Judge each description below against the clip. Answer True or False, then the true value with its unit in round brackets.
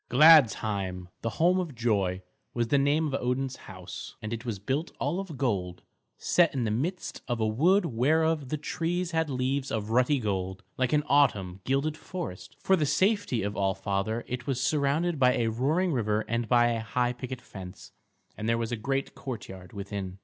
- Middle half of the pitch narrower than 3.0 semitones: False (5.6 semitones)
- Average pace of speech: True (190 wpm)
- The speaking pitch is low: True (125 Hz)